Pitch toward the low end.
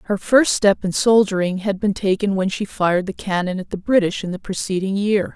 No: high, 195 Hz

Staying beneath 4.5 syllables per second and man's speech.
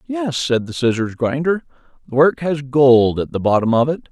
No: 5.0 syllables/s; male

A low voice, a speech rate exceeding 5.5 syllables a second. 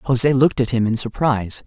Yes: low, 125 Hz; 6.0 syllables/s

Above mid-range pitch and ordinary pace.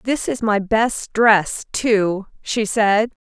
Yes: high, 215 Hz; average, 145 wpm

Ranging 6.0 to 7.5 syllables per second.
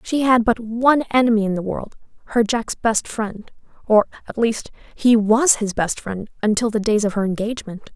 No: 5.0 syllables/s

